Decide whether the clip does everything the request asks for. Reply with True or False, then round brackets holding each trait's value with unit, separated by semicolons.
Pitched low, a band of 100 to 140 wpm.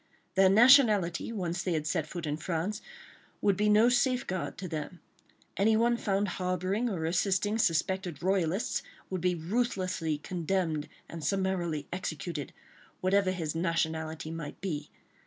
False (185 Hz; 135 wpm)